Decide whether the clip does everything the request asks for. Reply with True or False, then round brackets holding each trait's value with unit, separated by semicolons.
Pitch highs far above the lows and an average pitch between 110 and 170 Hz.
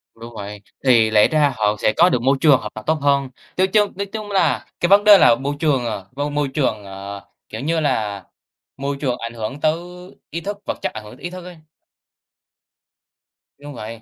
True (6.7 semitones; 135 Hz)